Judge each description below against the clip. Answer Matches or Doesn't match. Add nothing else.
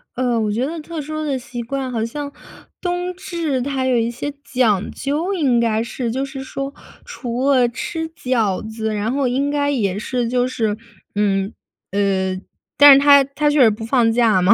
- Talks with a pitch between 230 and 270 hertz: Matches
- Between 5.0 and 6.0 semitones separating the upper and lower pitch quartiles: Doesn't match